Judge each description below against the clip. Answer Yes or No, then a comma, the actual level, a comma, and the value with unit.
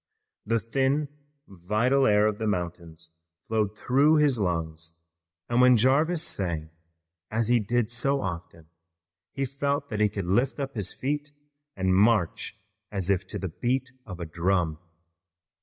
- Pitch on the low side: Yes, low, 105 Hz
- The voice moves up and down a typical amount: No, wide, 6.5 semitones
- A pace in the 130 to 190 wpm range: Yes, average, 150 wpm